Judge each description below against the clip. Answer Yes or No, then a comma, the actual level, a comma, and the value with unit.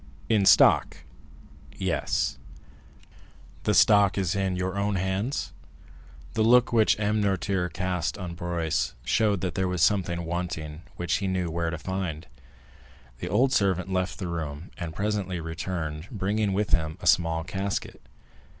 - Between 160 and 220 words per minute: No, average, 145 wpm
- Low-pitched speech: Yes, very low, 95 Hz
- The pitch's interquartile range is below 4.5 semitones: Yes, average, 3.0 semitones